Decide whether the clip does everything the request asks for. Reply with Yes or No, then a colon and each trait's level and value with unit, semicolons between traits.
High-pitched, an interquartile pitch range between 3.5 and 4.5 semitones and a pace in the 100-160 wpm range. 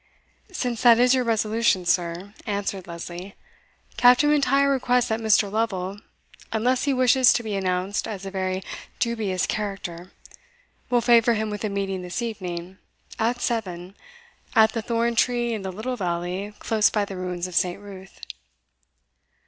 Yes: high, 210 Hz; average, 4.1 semitones; average, 155 wpm